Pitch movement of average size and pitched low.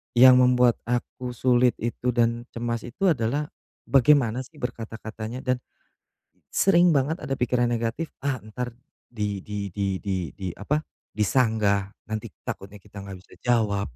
Yes: average, 3.3 semitones; low, 120 Hz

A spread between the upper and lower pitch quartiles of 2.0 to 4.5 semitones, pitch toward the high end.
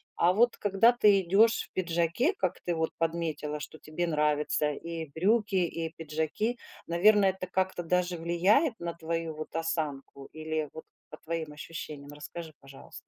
No: average, 3.2 semitones; medium, 165 Hz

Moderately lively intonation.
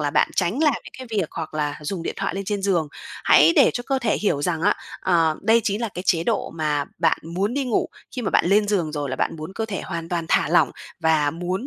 Yes: average, 4.6 semitones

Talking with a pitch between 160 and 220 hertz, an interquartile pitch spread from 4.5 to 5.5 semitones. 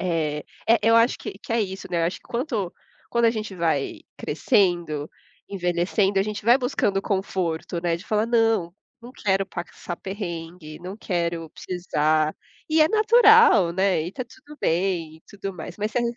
Yes: high, 190 Hz; average, 4.9 semitones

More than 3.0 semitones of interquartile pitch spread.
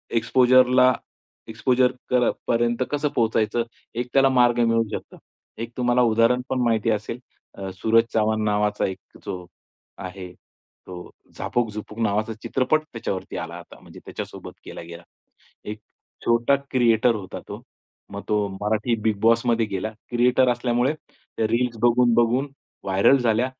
No: narrow, 2.5 semitones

